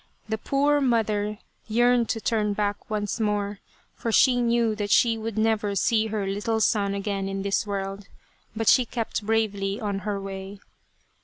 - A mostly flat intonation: Yes, narrow, 2.0 semitones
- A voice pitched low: No, high, 210 Hz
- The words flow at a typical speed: Yes, average, 165 wpm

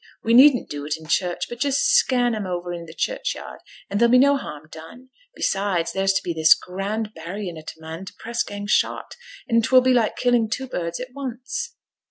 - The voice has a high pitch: Yes, high, 215 Hz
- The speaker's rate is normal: No, fast, 220 wpm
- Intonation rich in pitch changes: Yes, wide, 6.4 semitones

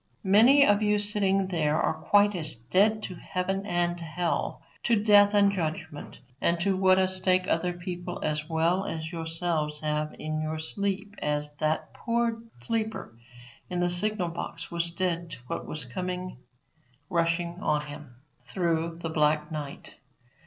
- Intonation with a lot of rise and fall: No, average, 3.8 semitones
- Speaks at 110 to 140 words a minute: No, average, 155 wpm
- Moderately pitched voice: Yes, medium, 175 Hz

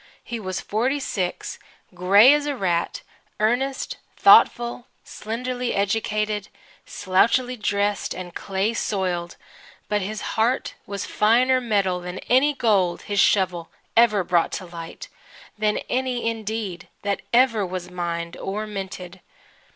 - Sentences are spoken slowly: Yes, slow, 125 wpm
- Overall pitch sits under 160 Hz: No, high, 210 Hz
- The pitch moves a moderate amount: Yes, average, 4.2 semitones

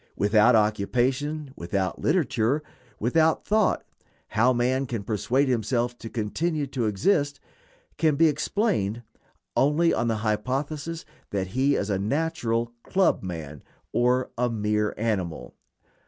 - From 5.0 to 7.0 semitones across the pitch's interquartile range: Yes, wide, 5.4 semitones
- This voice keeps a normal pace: No, slow, 125 wpm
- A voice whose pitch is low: Yes, low, 120 Hz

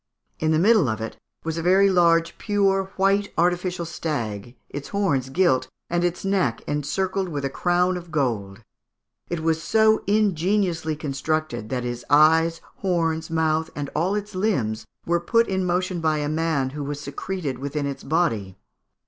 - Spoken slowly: No, average, 165 wpm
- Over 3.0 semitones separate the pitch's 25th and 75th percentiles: Yes, average, 4.5 semitones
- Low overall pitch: No, medium, 165 Hz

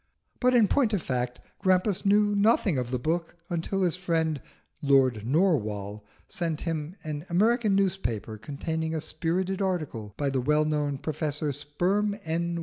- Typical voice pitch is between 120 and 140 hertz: No, medium, 160 Hz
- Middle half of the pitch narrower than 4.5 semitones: No, average, 5.3 semitones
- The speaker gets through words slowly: No, average, 150 wpm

